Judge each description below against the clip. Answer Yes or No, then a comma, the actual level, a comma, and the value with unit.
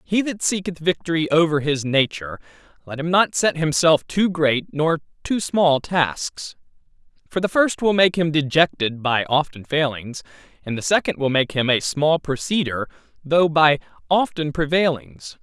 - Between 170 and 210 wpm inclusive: No, average, 160 wpm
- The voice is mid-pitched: Yes, medium, 155 Hz